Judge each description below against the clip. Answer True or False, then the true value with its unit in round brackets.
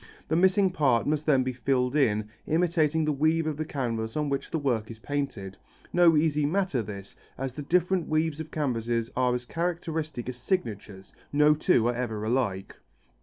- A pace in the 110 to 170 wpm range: False (180 wpm)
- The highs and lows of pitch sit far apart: False (4.8 semitones)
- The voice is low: False (145 Hz)